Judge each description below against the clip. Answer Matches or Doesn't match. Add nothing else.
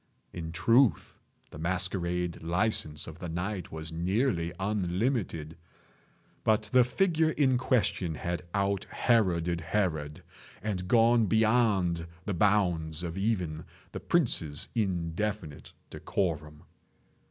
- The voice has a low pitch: Matches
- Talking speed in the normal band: Doesn't match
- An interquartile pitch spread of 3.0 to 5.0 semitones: Matches